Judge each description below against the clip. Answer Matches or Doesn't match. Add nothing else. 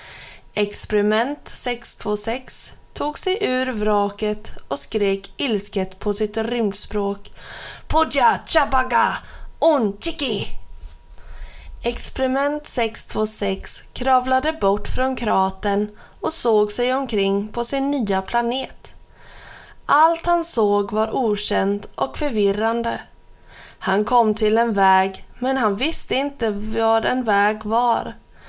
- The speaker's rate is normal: Doesn't match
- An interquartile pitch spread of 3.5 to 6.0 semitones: Matches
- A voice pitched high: Matches